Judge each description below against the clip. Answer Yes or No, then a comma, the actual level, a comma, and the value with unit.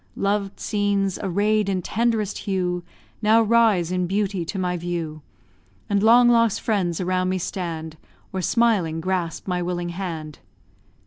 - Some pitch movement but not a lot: Yes, average, 3.1 semitones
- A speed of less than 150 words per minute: Yes, average, 140 wpm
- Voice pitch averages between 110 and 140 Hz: No, medium, 185 Hz